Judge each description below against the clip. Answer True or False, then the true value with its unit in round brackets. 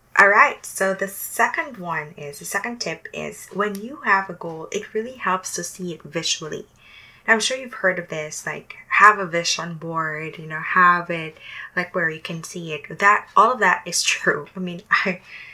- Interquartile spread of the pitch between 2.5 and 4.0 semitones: True (3.4 semitones)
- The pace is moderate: False (210 wpm)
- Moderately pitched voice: True (180 Hz)